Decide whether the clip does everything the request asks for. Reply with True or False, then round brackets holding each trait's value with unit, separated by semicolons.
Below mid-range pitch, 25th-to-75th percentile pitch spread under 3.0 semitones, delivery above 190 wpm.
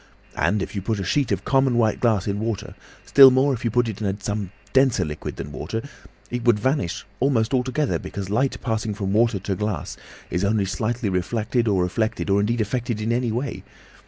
False (110 Hz; 3.3 semitones; 205 wpm)